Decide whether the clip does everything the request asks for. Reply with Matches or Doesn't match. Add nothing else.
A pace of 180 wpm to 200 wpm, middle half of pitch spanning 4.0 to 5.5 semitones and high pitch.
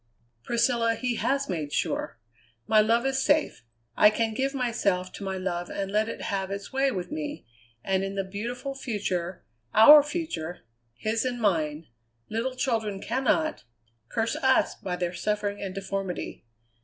Doesn't match